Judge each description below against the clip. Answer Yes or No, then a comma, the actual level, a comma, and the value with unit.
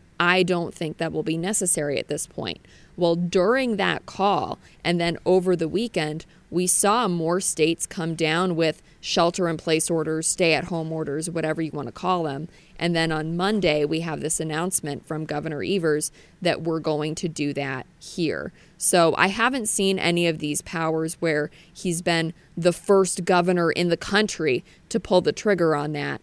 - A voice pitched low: No, medium, 170 Hz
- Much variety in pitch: No, narrow, 2.5 semitones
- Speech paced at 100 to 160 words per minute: No, average, 185 wpm